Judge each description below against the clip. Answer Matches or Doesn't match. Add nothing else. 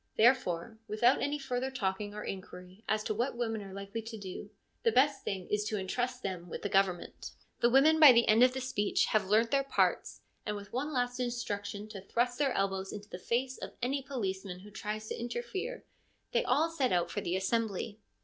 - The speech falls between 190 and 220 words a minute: Matches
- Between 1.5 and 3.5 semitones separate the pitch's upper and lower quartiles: Doesn't match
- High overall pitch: Matches